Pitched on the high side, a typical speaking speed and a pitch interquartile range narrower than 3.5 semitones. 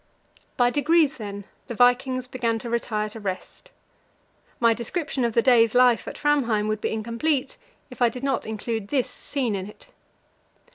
Yes: high, 240 Hz; average, 170 wpm; average, 3.0 semitones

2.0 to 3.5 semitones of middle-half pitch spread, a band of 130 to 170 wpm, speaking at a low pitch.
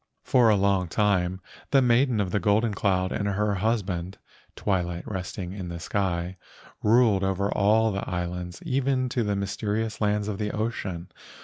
Yes: average, 2.9 semitones; average, 165 wpm; low, 100 Hz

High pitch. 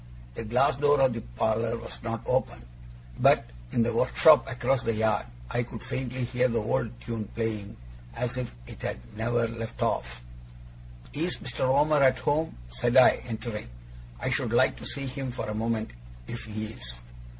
No: low, 115 Hz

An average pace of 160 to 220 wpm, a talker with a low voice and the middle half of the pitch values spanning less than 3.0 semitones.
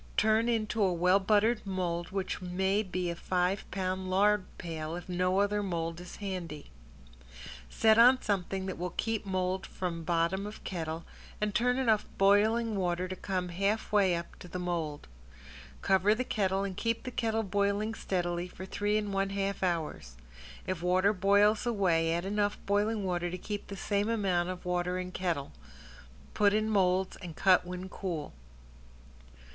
No: average, 170 wpm; high, 190 Hz; narrow, 2.6 semitones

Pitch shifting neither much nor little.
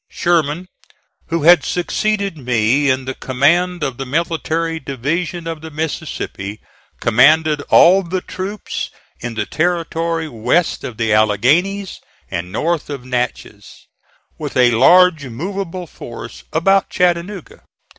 No: wide, 5.7 semitones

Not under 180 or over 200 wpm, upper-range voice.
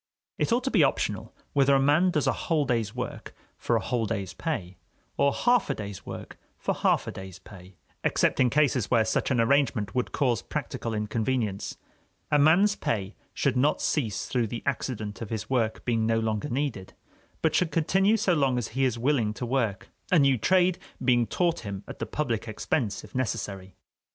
No: average, 195 wpm; low, 125 Hz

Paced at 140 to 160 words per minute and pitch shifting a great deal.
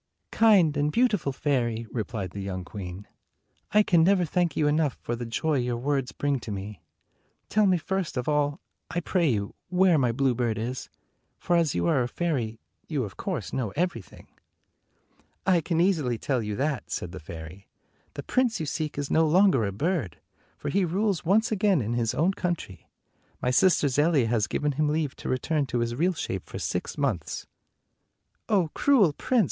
No: average, 185 wpm; wide, 6.9 semitones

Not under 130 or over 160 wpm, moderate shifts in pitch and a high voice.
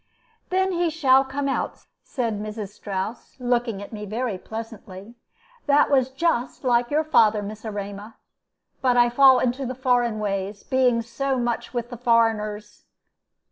Yes: average, 150 wpm; average, 3.6 semitones; high, 240 Hz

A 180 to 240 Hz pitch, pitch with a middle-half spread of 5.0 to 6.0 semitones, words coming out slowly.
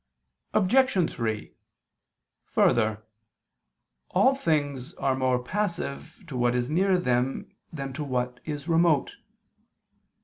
No: medium, 140 Hz; wide, 5.5 semitones; slow, 105 wpm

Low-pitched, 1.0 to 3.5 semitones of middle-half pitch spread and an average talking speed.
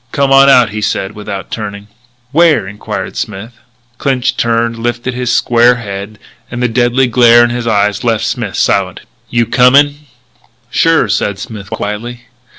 Yes: low, 120 Hz; average, 2.9 semitones; average, 155 wpm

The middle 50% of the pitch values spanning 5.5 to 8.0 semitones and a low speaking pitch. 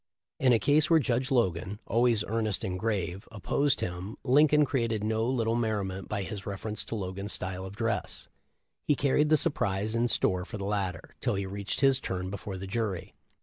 No: average, 4.0 semitones; low, 105 Hz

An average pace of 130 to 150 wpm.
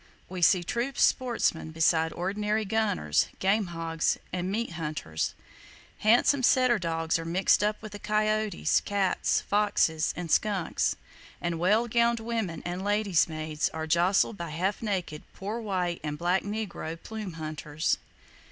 Yes: average, 140 wpm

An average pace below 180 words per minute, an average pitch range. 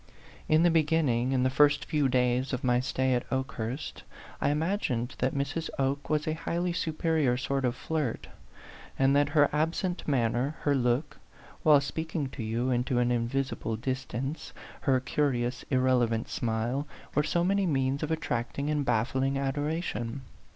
Yes: average, 155 wpm; average, 3.4 semitones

